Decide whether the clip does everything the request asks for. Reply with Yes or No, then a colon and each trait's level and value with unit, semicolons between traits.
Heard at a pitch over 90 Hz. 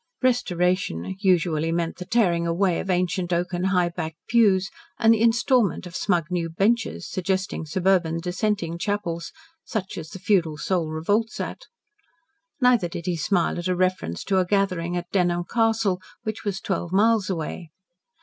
Yes: medium, 185 Hz